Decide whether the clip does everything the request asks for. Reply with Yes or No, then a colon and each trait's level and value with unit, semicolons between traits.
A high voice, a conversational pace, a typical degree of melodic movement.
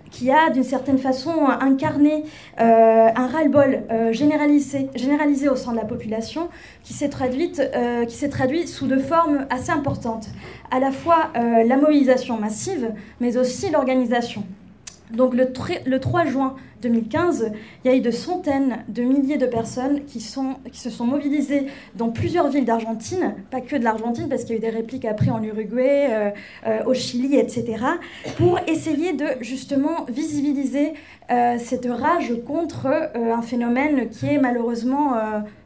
Yes: very high, 260 Hz; average, 170 wpm; average, 3.6 semitones